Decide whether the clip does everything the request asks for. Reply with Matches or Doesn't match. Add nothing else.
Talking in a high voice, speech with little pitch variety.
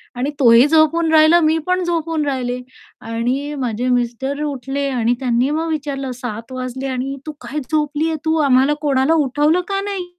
Doesn't match